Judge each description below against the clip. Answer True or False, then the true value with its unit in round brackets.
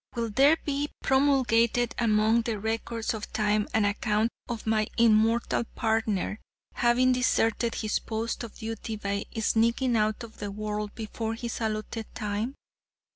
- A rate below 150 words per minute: True (140 wpm)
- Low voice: False (225 Hz)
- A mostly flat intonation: True (1.7 semitones)